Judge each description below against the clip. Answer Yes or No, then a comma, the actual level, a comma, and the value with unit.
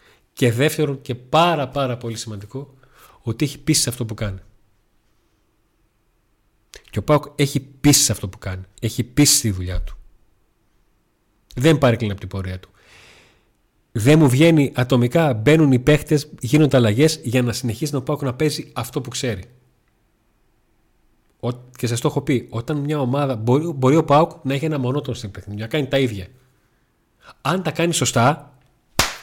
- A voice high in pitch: No, low, 125 Hz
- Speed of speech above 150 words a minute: Yes, average, 160 wpm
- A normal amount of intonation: Yes, average, 4.7 semitones